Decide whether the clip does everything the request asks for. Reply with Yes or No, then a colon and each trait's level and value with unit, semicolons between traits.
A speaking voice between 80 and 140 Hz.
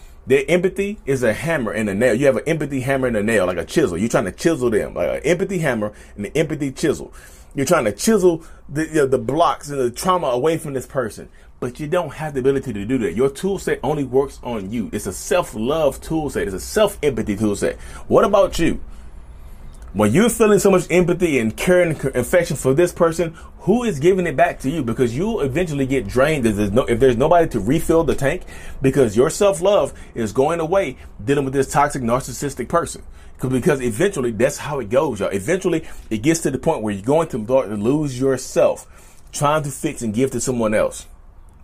Yes: low, 135 Hz